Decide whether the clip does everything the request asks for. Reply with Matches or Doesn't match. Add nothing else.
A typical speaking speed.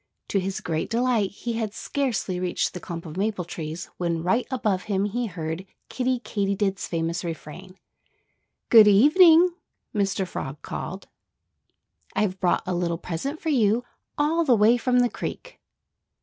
Matches